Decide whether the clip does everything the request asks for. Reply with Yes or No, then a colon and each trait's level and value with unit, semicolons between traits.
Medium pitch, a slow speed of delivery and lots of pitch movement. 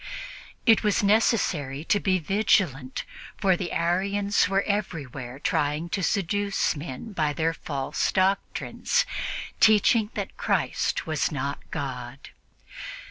Yes: medium, 175 Hz; slow, 115 wpm; wide, 6.0 semitones